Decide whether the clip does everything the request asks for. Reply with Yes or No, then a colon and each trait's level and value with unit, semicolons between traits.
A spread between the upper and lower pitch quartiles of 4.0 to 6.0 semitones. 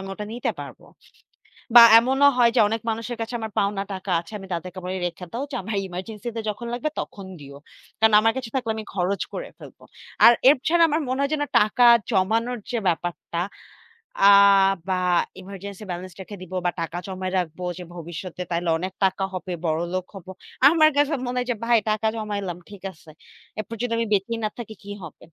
Yes: average, 4.3 semitones